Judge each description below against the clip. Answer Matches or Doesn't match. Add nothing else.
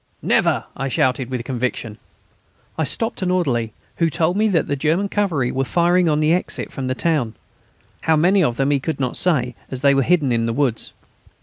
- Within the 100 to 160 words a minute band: Doesn't match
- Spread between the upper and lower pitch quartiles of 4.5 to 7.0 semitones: Matches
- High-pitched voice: Doesn't match